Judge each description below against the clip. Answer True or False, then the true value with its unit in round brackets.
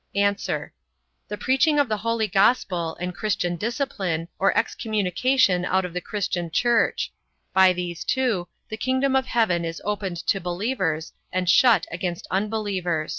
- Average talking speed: True (145 wpm)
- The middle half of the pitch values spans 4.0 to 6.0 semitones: True (4.5 semitones)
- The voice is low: False (195 Hz)